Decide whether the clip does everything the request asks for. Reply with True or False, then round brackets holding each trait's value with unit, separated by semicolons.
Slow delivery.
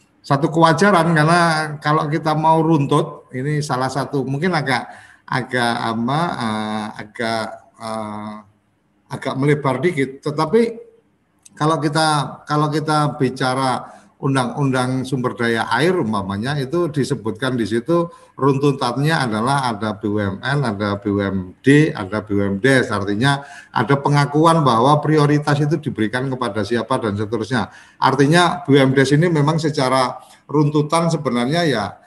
False (110 wpm)